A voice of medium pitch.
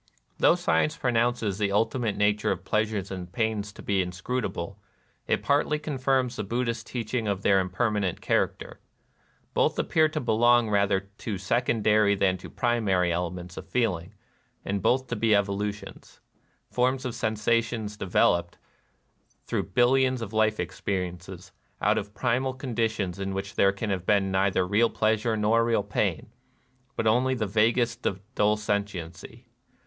No: low, 105 Hz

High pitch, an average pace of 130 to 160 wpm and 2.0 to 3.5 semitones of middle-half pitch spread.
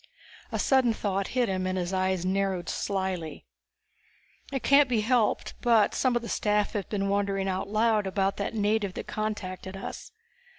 No: high, 200 Hz; average, 170 wpm; average, 2.7 semitones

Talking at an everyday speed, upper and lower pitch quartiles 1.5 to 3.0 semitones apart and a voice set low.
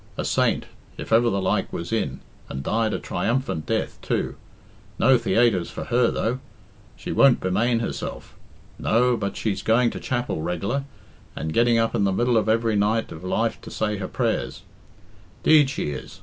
No: average, 175 wpm; average, 3.5 semitones; low, 115 Hz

